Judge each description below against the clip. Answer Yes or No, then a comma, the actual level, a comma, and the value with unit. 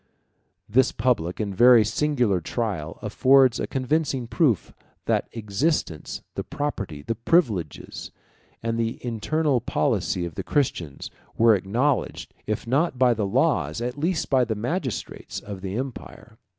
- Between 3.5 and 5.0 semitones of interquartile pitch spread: Yes, average, 4.7 semitones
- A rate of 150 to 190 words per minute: No, average, 140 wpm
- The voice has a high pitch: No, low, 115 Hz